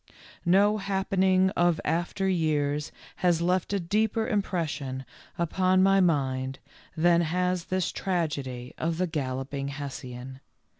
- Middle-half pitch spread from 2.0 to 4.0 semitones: No, average, 4.7 semitones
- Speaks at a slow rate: Yes, slow, 115 wpm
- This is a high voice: No, medium, 170 Hz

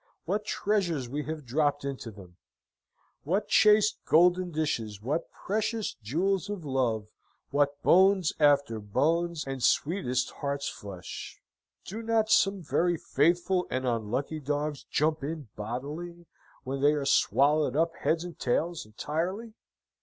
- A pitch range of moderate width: Yes, average, 4.9 semitones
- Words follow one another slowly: Yes, slow, 130 wpm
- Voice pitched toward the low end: No, medium, 150 Hz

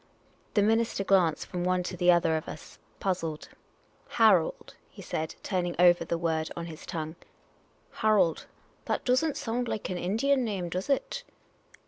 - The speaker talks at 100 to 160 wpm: No, average, 175 wpm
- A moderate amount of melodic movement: Yes, average, 4.5 semitones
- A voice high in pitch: No, medium, 180 Hz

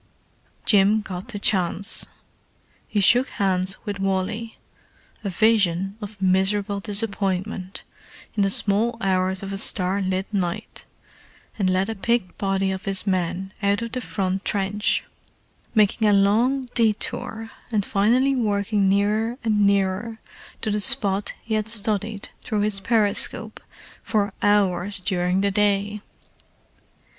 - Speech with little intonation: Yes, narrow, 2.0 semitones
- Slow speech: Yes, slow, 125 wpm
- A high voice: Yes, high, 200 Hz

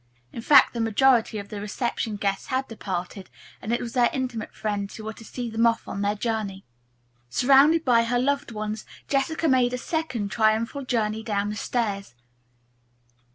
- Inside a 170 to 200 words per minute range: Yes, average, 175 wpm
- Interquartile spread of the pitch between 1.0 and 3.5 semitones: Yes, average, 3.2 semitones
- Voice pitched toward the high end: Yes, high, 230 Hz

